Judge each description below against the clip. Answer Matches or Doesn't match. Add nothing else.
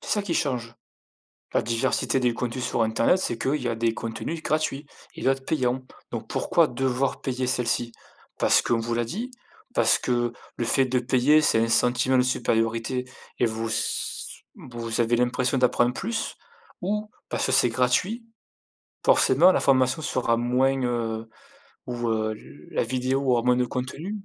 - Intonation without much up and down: Matches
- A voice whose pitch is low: Matches